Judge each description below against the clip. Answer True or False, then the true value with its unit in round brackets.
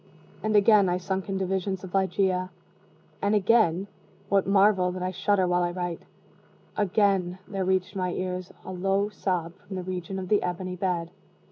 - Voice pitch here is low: False (185 Hz)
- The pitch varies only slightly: True (1.5 semitones)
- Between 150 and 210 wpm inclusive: True (170 wpm)